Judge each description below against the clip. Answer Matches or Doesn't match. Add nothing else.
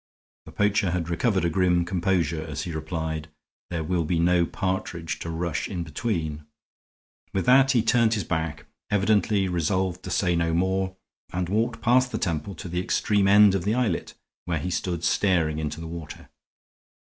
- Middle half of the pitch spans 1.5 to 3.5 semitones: Matches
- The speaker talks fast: Doesn't match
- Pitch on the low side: Matches